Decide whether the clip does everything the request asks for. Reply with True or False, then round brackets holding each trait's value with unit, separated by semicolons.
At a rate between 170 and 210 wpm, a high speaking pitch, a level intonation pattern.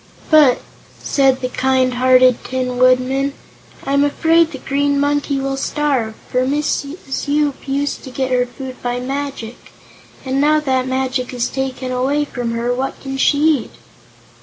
False (160 wpm; 265 Hz; 2.0 semitones)